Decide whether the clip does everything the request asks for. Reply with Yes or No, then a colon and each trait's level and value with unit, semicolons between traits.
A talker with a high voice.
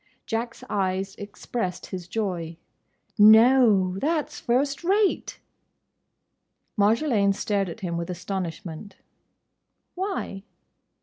Yes: high, 200 Hz